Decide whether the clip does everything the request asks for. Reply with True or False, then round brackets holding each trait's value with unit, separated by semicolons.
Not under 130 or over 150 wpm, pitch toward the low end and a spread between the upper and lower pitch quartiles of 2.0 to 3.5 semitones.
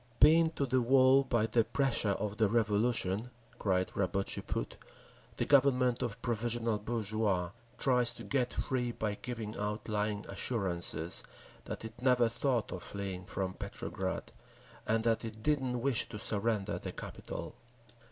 True (145 wpm; 115 Hz; 3.1 semitones)